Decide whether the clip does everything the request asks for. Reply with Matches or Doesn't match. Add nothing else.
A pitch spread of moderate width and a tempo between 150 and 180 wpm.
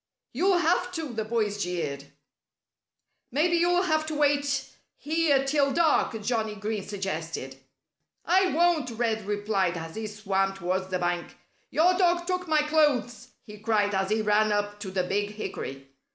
Doesn't match